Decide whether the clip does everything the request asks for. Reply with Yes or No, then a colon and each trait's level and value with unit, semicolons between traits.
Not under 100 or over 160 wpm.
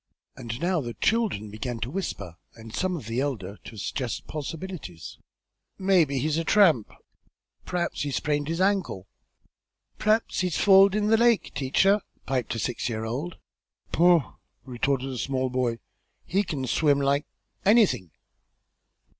Yes: average, 145 wpm